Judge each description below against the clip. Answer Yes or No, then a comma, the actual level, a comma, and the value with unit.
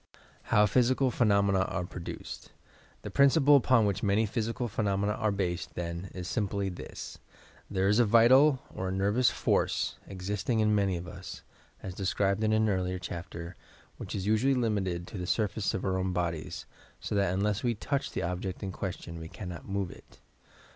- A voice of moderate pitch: No, low, 100 Hz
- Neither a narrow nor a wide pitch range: Yes, average, 3.0 semitones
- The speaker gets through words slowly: No, average, 180 wpm